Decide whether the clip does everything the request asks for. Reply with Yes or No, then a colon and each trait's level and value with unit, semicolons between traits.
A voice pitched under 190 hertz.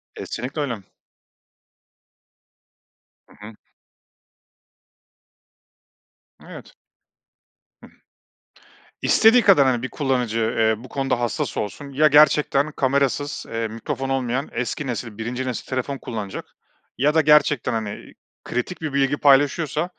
Yes: low, 135 Hz